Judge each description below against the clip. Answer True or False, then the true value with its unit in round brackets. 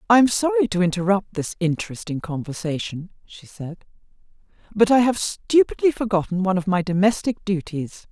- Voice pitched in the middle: False (195 Hz)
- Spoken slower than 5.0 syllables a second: False (5.4 syllables/s)